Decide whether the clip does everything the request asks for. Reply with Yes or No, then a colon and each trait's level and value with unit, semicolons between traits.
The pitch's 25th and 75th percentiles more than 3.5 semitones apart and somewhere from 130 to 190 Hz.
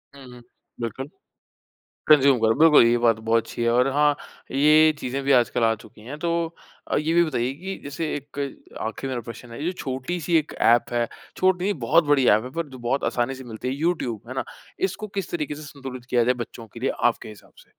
Yes: average, 4.2 semitones; low, 135 Hz